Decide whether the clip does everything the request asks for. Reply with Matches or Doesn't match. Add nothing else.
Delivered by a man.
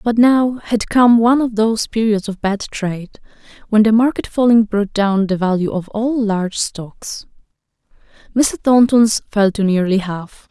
Doesn't match